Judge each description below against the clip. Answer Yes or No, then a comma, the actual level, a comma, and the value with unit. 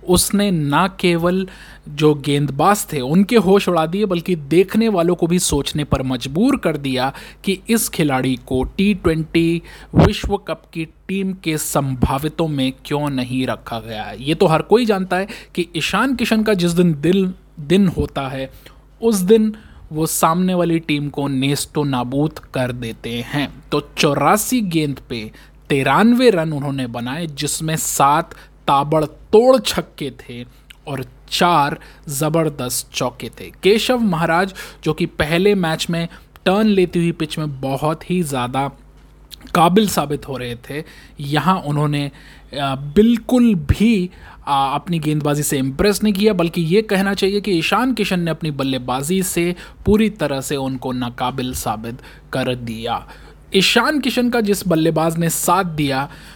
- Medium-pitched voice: Yes, medium, 160 Hz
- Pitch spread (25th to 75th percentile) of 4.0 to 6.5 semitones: Yes, wide, 5.5 semitones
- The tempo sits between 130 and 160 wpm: Yes, average, 150 wpm